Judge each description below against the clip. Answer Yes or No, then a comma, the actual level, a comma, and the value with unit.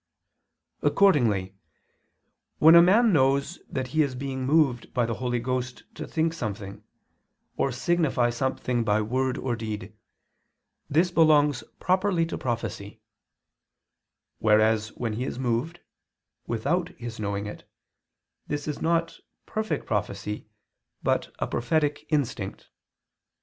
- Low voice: Yes, low, 130 Hz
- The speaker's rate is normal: No, slow, 120 wpm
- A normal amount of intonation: No, wide, 5.8 semitones